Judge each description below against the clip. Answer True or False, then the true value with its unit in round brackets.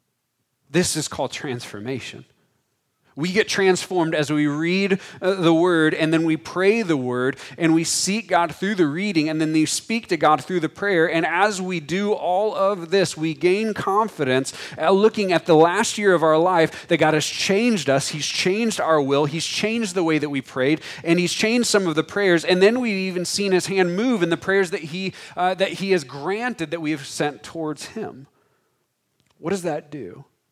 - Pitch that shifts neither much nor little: True (4.0 semitones)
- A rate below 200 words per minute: False (205 wpm)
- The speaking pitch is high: False (170 Hz)